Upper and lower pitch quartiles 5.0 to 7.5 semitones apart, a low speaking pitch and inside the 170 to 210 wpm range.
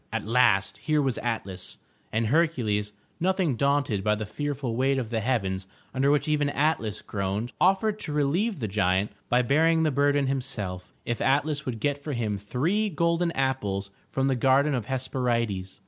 Yes: wide, 5.5 semitones; low, 130 Hz; average, 175 wpm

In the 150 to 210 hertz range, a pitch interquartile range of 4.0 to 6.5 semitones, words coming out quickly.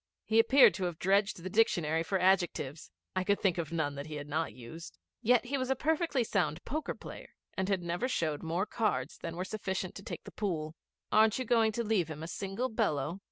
Yes: medium, 185 Hz; average, 5.3 semitones; fast, 215 wpm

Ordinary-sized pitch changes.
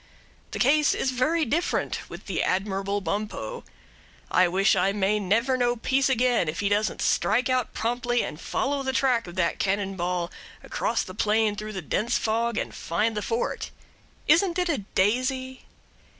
Yes: average, 4.7 semitones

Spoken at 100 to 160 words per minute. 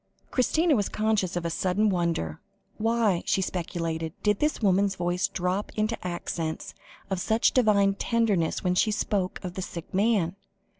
Yes: average, 155 wpm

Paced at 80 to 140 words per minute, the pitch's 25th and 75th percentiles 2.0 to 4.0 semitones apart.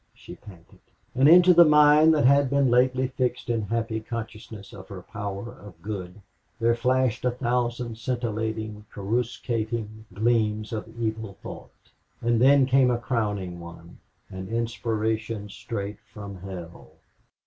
Yes: slow, 135 wpm; average, 3.3 semitones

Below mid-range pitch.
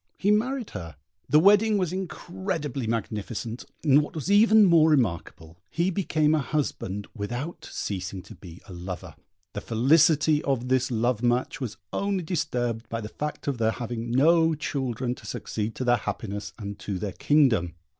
Yes: low, 125 Hz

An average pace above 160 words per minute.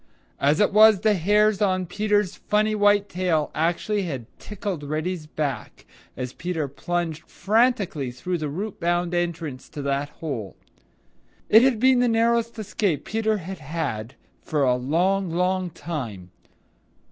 No: average, 145 wpm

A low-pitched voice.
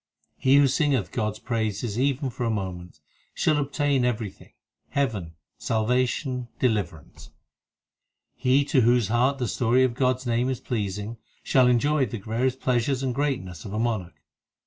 Yes: low, 120 Hz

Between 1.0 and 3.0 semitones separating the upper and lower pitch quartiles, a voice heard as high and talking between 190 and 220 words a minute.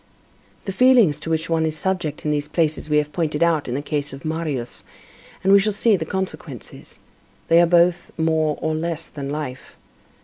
No: narrow, 2.4 semitones; medium, 160 Hz; average, 195 wpm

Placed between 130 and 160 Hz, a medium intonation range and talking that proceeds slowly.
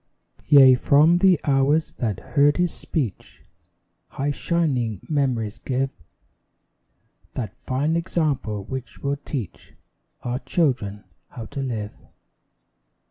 Yes: low, 135 Hz; average, 3.8 semitones; slow, 105 wpm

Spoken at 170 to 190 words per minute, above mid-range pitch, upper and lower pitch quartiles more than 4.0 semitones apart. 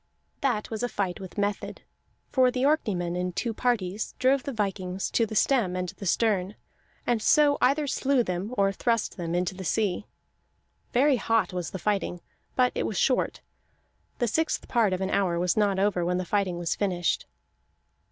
Yes: average, 180 wpm; high, 205 Hz; average, 4.9 semitones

